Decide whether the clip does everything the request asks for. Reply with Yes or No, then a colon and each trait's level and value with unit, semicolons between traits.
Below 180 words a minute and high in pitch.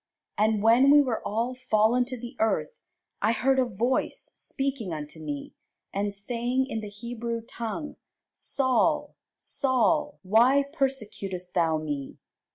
Yes: slow, 135 wpm; high, 230 Hz